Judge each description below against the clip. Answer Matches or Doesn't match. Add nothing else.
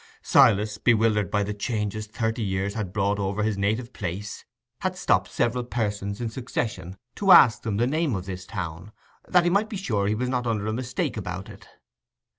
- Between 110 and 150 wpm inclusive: Doesn't match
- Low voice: Matches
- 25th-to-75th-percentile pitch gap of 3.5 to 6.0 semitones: Doesn't match